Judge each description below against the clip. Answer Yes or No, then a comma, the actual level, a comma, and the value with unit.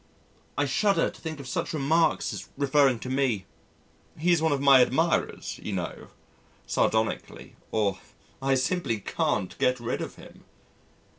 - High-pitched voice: No, low, 135 Hz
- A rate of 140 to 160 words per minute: Yes, average, 145 wpm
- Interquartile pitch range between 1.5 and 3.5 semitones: No, average, 4.7 semitones